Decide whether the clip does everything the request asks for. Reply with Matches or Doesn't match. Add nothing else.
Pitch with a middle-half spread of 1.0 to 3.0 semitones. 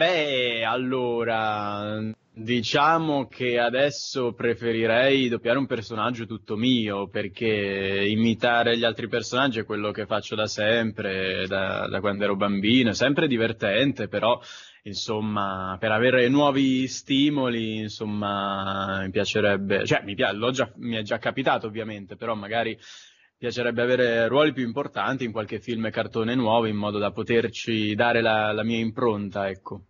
Matches